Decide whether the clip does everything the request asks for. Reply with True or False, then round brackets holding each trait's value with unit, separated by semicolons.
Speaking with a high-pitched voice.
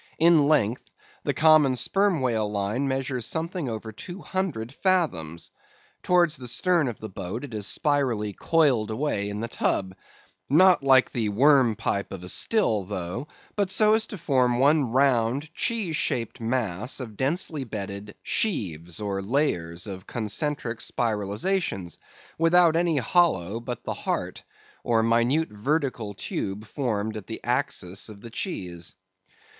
False (120 Hz)